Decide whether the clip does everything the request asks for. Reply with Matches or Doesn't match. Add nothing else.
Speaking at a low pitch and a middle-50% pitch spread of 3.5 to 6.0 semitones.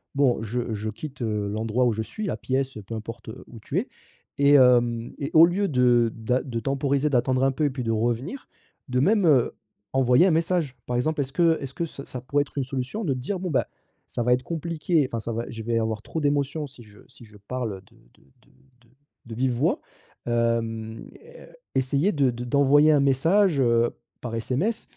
Matches